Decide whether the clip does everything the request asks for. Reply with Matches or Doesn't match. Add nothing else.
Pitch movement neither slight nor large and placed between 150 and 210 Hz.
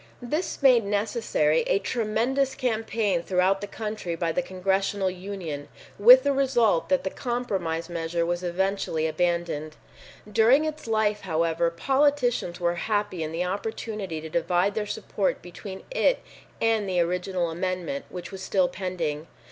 Matches